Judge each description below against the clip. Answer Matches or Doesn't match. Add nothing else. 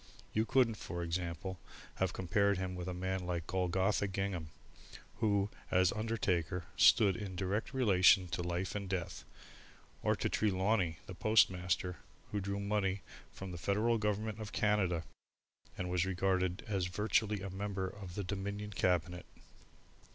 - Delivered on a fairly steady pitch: Matches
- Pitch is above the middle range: Doesn't match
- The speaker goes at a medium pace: Matches